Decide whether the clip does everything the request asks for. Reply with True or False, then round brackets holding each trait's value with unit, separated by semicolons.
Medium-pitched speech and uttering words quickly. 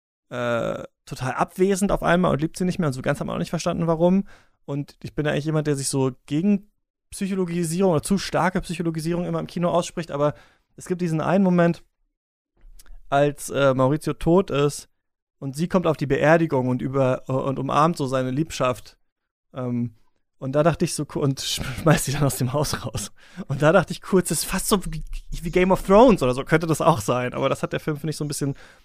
True (155 Hz; 225 wpm)